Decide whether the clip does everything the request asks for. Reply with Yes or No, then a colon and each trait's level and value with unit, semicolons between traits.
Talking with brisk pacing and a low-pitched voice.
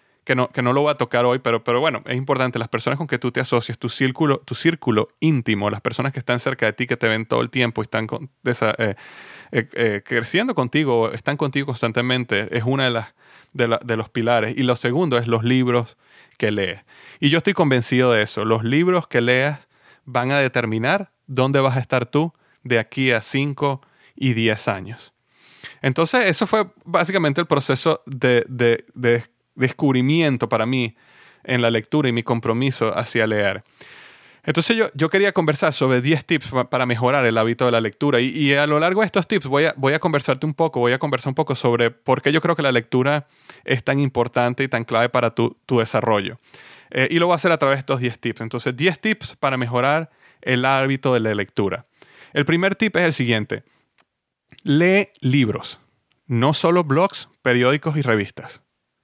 Yes: fast, 205 wpm; low, 130 Hz